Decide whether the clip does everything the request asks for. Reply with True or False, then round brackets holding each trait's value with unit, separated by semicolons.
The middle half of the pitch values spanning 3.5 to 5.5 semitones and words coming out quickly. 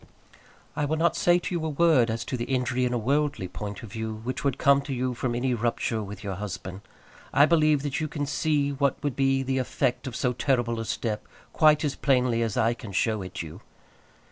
True (3.9 semitones; 225 wpm)